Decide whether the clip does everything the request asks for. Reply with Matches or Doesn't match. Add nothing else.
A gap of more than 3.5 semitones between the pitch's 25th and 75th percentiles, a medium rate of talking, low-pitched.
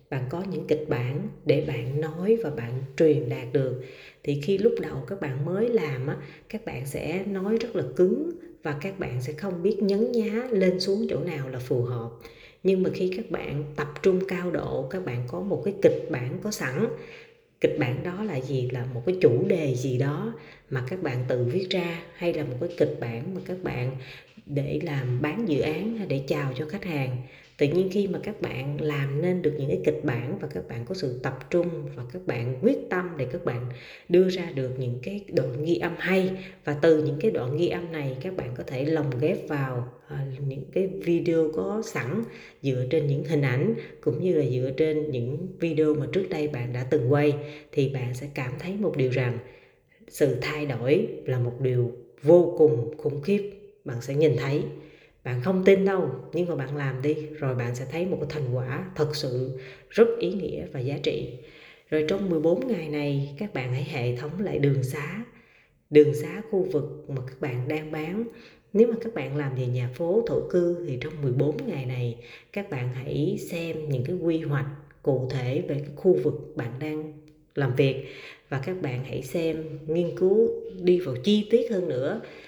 Doesn't match